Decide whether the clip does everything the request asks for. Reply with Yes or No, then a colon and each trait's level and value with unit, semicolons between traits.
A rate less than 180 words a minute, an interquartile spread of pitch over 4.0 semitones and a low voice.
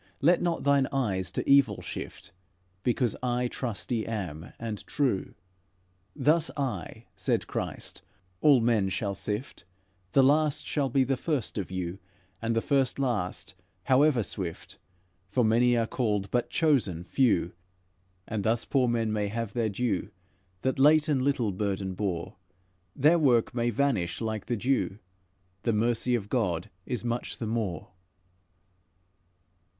Yes: average, 145 wpm; average, 4.7 semitones; low, 115 Hz